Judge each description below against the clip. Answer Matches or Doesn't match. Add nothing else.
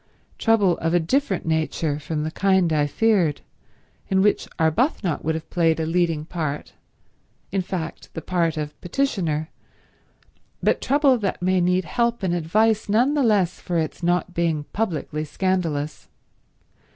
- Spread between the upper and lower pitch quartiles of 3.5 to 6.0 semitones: Matches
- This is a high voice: Doesn't match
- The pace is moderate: Matches